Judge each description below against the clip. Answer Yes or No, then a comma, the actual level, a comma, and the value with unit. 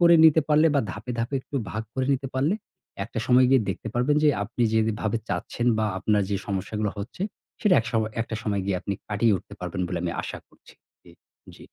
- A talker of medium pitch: No, low, 110 Hz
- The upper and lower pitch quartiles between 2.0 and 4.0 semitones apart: No, average, 4.5 semitones